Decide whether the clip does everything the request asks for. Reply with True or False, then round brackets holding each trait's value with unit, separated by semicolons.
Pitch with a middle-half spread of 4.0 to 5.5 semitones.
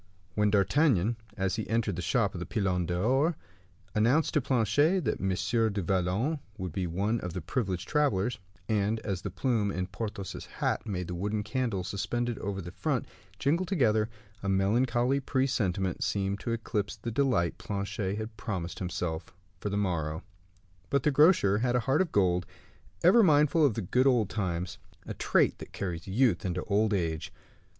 True (4.9 semitones)